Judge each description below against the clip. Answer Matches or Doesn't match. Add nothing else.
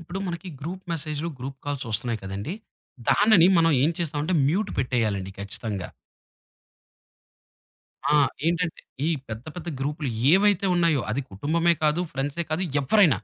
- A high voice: Doesn't match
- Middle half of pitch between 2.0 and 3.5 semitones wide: Doesn't match